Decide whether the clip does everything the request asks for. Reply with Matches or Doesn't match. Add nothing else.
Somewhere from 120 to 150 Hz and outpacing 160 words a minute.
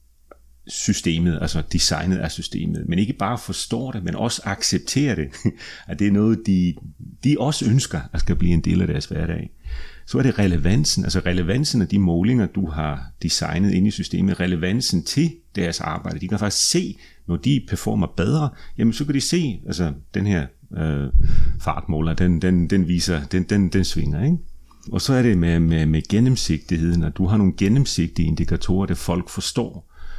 Doesn't match